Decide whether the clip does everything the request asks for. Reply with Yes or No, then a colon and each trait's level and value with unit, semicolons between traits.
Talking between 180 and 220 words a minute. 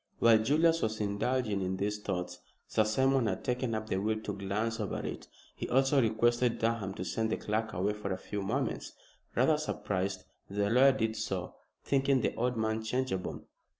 Yes: average, 185 wpm